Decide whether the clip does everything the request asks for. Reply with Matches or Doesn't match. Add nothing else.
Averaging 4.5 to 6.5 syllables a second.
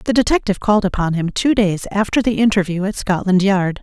Matches